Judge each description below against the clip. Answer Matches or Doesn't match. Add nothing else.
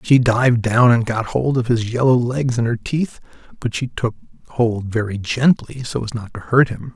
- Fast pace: Matches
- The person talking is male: Matches